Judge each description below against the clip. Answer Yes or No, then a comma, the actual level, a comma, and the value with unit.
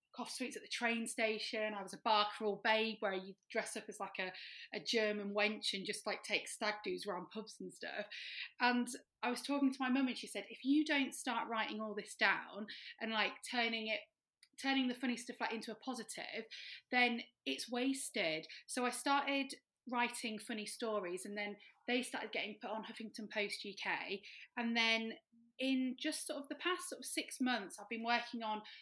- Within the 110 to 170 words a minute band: No, average, 200 wpm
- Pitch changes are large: No, average, 3.1 semitones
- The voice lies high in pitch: Yes, high, 225 Hz